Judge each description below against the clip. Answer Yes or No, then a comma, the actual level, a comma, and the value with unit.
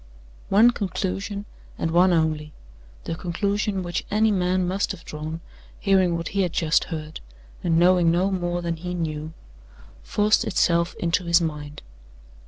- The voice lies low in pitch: No, medium, 175 Hz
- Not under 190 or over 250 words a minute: No, average, 150 wpm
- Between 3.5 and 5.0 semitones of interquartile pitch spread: No, average, 2.7 semitones